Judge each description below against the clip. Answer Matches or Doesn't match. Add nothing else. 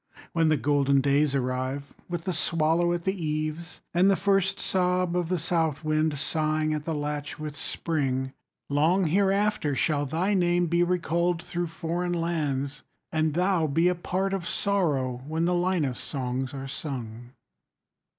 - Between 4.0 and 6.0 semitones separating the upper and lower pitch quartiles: Doesn't match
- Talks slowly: Doesn't match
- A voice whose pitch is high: Doesn't match